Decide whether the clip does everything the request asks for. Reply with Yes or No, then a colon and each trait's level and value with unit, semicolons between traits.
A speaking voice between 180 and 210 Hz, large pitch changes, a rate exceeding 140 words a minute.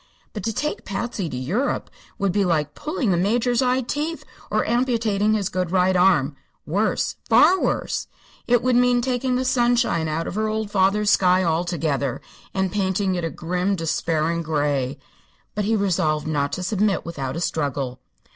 Yes: high, 190 Hz; wide, 5.7 semitones; average, 170 wpm